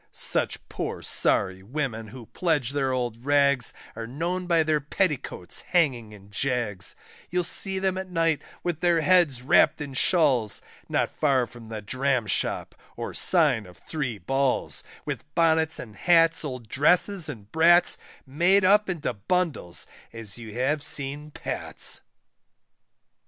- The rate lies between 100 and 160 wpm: Yes, average, 145 wpm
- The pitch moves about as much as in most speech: No, wide, 5.9 semitones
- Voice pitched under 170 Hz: Yes, medium, 140 Hz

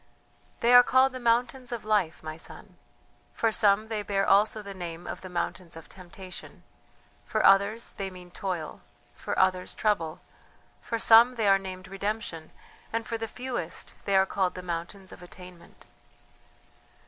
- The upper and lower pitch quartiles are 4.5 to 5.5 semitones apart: No, average, 3.7 semitones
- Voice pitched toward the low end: No, high, 195 Hz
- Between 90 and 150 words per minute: No, average, 160 wpm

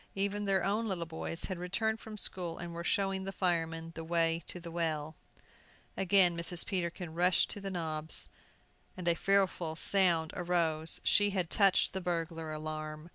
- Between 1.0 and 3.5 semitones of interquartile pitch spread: Yes, average, 2.9 semitones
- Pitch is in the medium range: Yes, medium, 175 Hz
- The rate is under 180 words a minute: Yes, average, 170 wpm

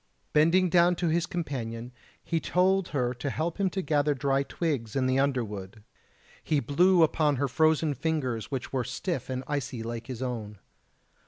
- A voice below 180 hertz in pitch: Yes, medium, 140 Hz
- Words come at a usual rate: Yes, average, 170 wpm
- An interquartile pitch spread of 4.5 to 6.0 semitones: Yes, average, 4.9 semitones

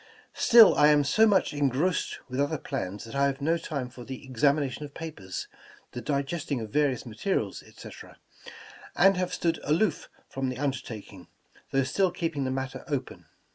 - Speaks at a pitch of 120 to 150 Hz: Yes, medium, 140 Hz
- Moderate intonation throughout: Yes, average, 4.1 semitones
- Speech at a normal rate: Yes, average, 170 wpm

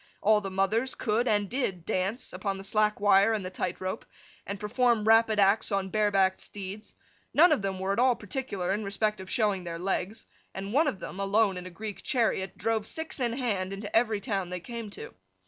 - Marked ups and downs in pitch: No, average, 2.7 semitones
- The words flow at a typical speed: No, fast, 215 wpm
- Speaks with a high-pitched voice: Yes, high, 205 Hz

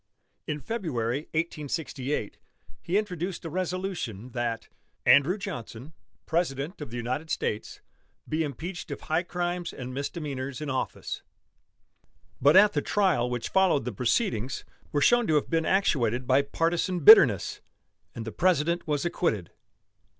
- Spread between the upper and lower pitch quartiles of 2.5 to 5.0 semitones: No, wide, 5.6 semitones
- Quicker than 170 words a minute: No, slow, 135 wpm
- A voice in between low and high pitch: Yes, medium, 150 Hz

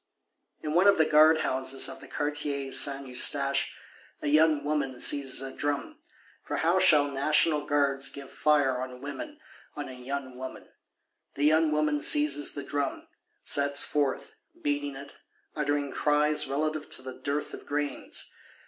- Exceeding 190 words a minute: No, average, 150 wpm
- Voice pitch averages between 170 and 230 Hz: No, medium, 145 Hz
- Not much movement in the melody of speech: Yes, narrow, 1.7 semitones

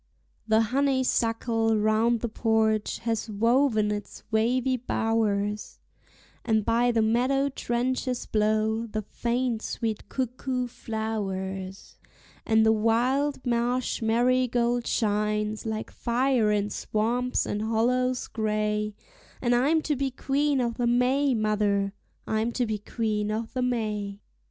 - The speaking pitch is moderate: No, high, 225 Hz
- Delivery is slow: Yes, slow, 120 wpm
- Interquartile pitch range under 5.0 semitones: Yes, narrow, 2.6 semitones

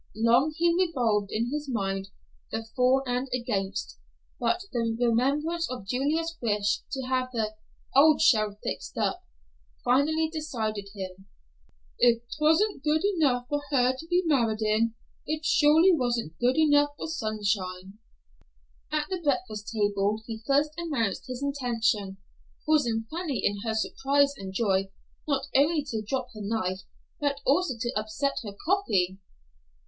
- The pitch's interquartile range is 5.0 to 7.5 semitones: Yes, wide, 5.5 semitones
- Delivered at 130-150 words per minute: Yes, average, 145 wpm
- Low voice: No, very high, 250 Hz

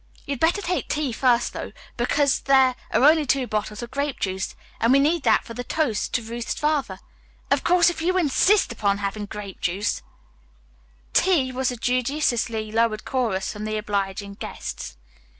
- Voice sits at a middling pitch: No, high, 240 Hz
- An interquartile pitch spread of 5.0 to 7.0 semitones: Yes, average, 5.3 semitones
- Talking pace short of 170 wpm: No, average, 175 wpm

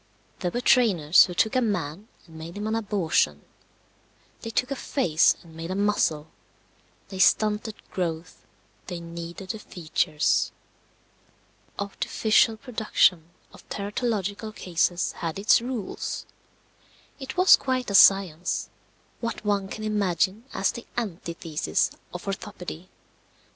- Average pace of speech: No, slow, 125 wpm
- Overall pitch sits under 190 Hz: No, high, 195 Hz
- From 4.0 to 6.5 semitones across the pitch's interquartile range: Yes, average, 4.5 semitones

